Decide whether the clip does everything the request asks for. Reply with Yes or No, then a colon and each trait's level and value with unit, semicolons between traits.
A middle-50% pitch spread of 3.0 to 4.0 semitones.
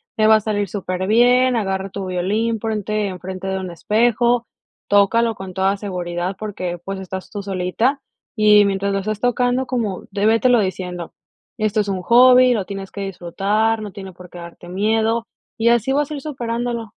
Yes: average, 3.4 semitones